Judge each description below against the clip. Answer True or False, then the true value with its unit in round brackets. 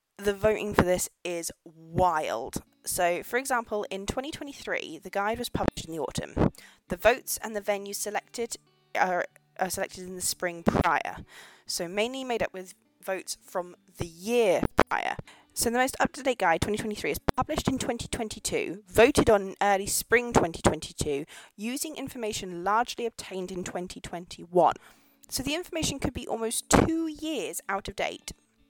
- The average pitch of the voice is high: True (205 Hz)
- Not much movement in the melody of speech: False (4.7 semitones)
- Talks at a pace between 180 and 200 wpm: False (155 wpm)